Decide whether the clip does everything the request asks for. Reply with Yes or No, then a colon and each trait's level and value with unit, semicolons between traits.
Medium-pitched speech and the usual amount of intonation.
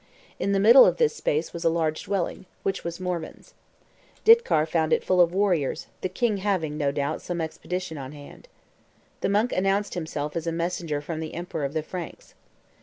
Yes: medium, 170 Hz; average, 3.7 semitones